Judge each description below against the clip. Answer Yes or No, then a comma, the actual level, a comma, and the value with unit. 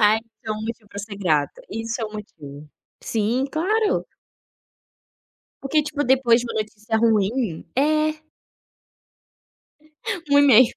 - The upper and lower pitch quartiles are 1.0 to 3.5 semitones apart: No, average, 4.2 semitones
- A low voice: No, high, 225 Hz